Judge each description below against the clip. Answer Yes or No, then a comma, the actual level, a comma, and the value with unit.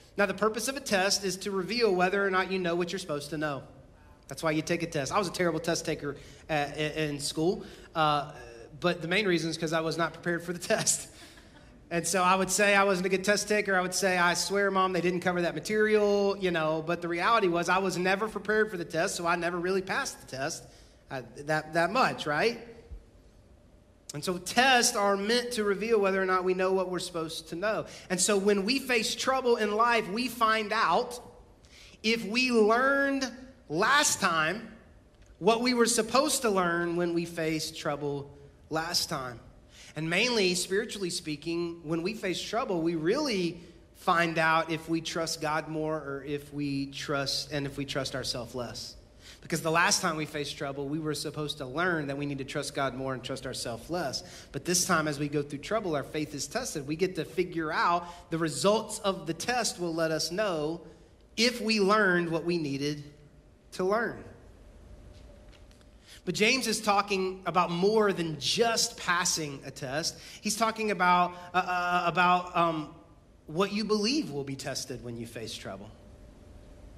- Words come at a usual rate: Yes, average, 195 wpm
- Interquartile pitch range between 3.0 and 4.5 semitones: No, average, 5.1 semitones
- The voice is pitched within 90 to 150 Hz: No, medium, 170 Hz